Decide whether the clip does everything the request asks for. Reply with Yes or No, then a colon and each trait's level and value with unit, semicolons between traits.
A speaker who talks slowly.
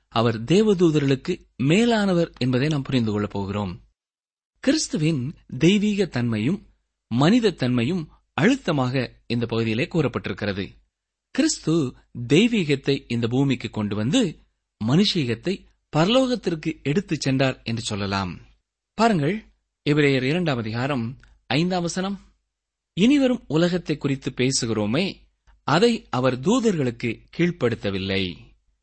No: average, 90 wpm